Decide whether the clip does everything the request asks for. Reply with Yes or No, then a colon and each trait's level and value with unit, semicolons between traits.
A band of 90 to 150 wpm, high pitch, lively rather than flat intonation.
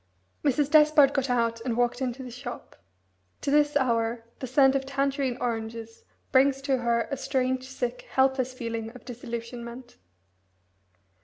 No: average, 145 wpm; very high, 255 Hz; narrow, 2.5 semitones